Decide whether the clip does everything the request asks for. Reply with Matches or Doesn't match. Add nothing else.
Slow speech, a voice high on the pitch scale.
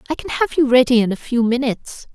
Doesn't match